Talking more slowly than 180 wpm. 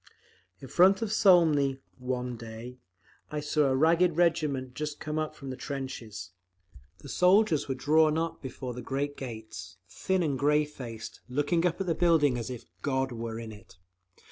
Yes: average, 170 wpm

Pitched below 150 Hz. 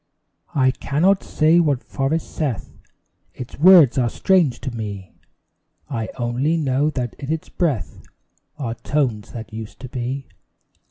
Yes: low, 135 Hz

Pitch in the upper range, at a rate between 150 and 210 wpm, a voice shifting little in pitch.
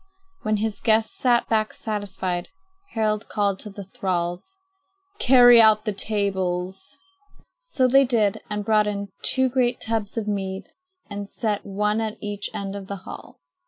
Yes: high, 210 Hz; average, 155 wpm; narrow, 2.1 semitones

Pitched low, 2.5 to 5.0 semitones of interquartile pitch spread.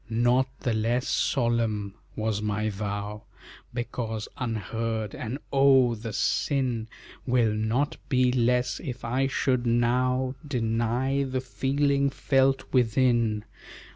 Yes: low, 120 Hz; average, 2.8 semitones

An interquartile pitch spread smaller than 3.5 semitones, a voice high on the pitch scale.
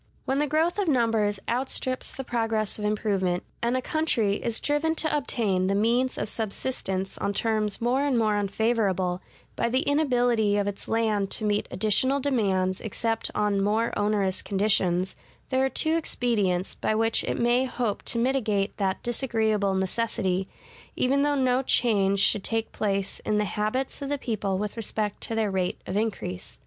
No: average, 3.9 semitones; high, 220 Hz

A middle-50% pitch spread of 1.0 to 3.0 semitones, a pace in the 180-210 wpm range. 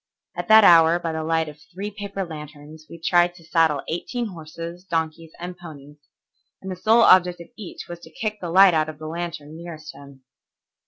Yes: narrow, 2.5 semitones; average, 200 wpm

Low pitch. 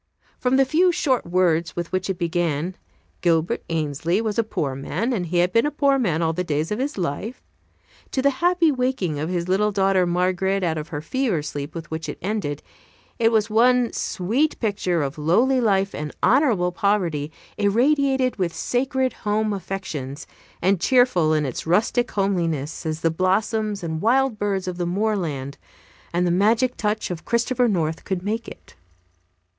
No: high, 190 Hz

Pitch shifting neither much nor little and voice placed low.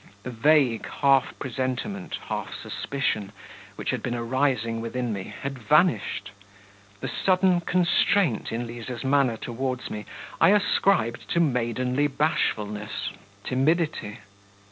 Yes: average, 4.7 semitones; low, 130 Hz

